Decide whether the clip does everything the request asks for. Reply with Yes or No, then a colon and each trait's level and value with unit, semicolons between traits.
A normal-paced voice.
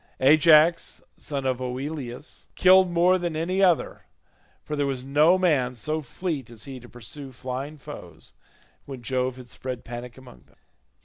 Yes: average, 160 wpm